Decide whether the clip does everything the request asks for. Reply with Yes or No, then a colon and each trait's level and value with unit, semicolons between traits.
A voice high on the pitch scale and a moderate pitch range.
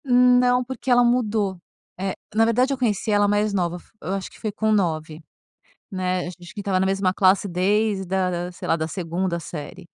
Yes: high, 195 Hz; average, 3.3 semitones